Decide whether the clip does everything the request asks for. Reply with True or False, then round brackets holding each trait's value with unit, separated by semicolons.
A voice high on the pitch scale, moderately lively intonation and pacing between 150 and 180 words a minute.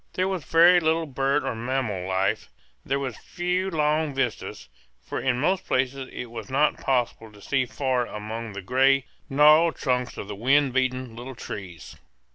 False (130 Hz; 4.2 semitones; 170 wpm)